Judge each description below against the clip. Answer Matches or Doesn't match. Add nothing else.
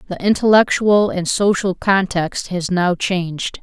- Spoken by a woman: Matches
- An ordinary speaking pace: Doesn't match